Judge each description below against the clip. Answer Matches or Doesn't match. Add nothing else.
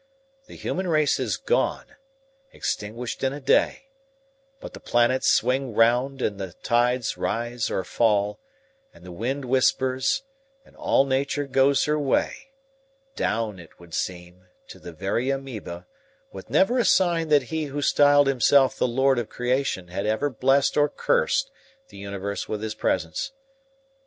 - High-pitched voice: Doesn't match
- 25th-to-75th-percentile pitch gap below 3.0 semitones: Doesn't match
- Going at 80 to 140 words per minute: Doesn't match